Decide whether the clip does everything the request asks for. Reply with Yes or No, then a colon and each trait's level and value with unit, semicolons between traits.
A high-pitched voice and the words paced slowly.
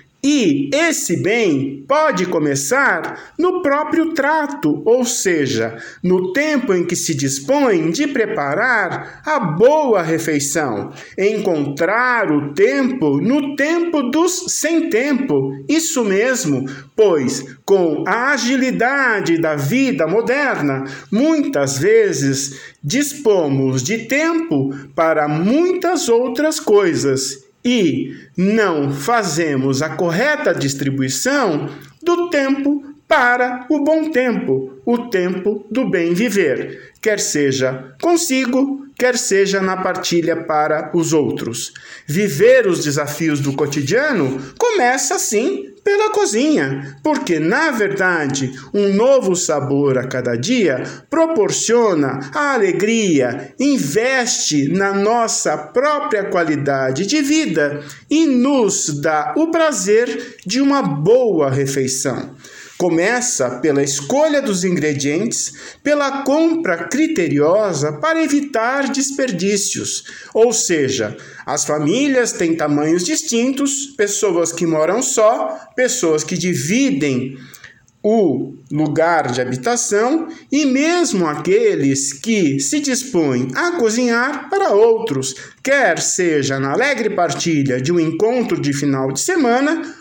Yes: high, 220 Hz; slow, 105 wpm